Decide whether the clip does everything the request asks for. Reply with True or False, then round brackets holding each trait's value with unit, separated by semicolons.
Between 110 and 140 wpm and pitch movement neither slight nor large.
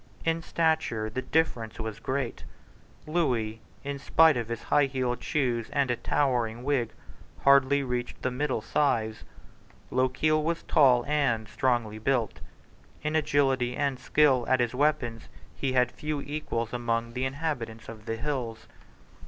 True (135 wpm; 3.6 semitones)